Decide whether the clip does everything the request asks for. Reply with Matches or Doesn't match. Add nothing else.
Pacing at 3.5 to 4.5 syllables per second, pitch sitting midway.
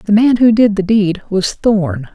Doesn't match